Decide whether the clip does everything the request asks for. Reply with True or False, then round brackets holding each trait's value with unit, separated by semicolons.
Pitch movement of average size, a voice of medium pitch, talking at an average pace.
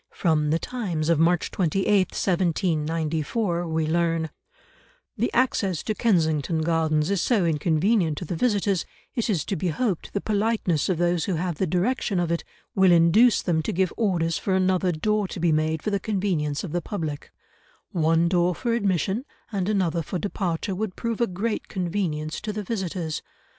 True (3.8 semitones; 175 Hz; 175 wpm)